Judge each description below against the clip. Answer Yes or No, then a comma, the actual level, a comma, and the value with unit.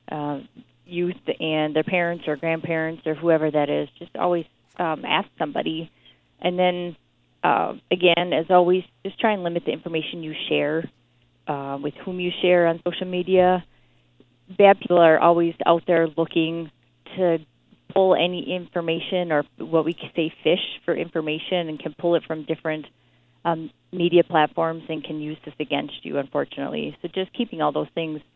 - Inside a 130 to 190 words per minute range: Yes, average, 165 wpm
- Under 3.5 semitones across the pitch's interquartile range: Yes, narrow, 2.6 semitones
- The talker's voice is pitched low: No, medium, 165 Hz